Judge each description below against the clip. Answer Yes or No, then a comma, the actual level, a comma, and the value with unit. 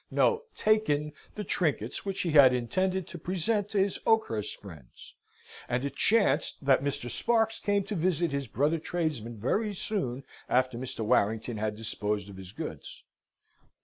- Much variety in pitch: Yes, wide, 8.7 semitones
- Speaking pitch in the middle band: Yes, medium, 145 Hz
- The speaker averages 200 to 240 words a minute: No, average, 155 wpm